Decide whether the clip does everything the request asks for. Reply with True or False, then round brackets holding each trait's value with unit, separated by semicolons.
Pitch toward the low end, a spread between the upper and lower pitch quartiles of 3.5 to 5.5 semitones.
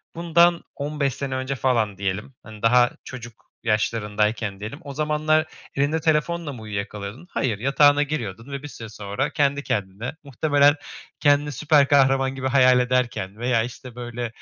True (130 Hz; 4.4 semitones)